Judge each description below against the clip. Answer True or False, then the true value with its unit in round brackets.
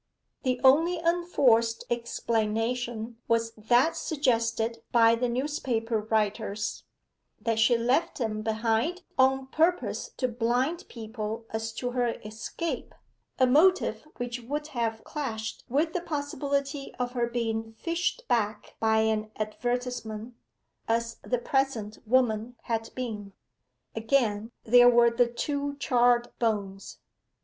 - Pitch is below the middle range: False (235 Hz)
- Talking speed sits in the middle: False (120 wpm)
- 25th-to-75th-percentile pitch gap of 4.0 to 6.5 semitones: False (3.1 semitones)